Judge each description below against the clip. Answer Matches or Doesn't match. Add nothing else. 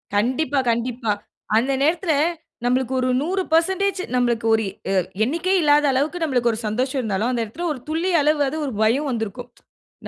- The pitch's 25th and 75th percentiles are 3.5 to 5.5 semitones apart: Matches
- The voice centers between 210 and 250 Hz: Doesn't match